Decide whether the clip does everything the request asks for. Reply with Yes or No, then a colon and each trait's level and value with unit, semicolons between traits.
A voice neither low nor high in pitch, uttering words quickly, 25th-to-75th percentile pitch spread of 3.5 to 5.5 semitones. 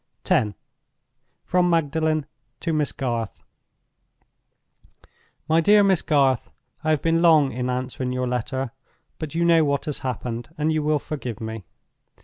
No: medium, 145 Hz; average, 140 wpm; average, 4.1 semitones